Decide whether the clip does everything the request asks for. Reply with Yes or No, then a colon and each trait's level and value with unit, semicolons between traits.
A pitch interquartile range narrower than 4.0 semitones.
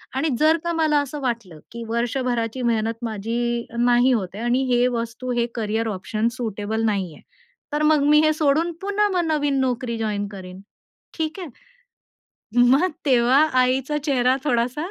No: average, 4.3 semitones